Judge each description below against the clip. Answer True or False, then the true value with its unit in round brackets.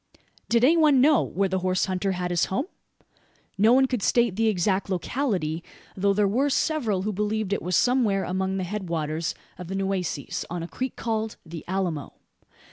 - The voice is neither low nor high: False (195 Hz)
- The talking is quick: False (190 wpm)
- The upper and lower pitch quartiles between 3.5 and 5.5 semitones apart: True (3.9 semitones)